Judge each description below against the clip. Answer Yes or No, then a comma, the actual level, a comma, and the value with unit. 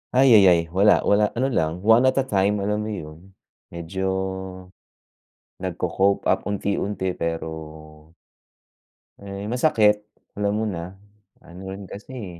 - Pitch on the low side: Yes, very low, 95 Hz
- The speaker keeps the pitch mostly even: No, average, 3.0 semitones